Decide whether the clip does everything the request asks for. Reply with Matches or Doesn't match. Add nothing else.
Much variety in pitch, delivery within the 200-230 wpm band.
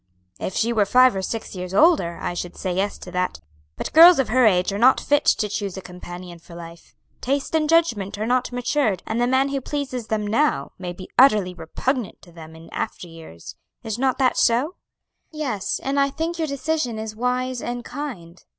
Matches